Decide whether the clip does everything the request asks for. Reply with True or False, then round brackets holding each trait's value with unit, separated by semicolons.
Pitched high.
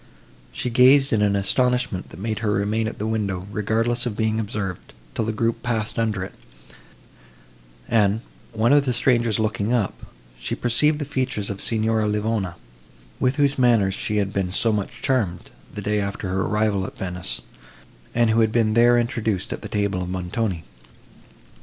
False (110 Hz)